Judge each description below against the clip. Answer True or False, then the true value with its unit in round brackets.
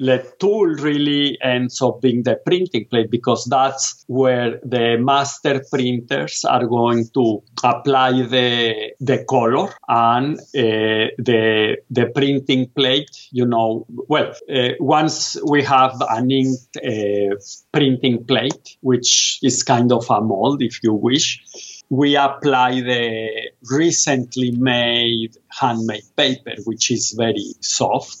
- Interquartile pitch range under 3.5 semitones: True (2.7 semitones)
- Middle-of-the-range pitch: False (125 Hz)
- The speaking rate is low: True (130 wpm)